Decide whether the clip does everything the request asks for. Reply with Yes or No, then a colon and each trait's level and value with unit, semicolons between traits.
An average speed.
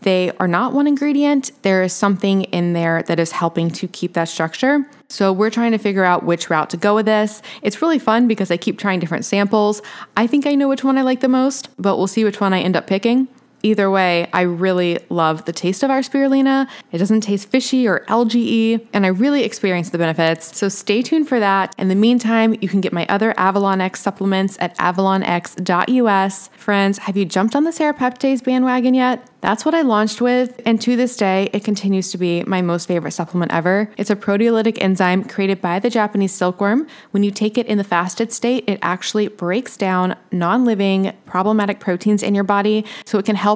No: fast, 215 wpm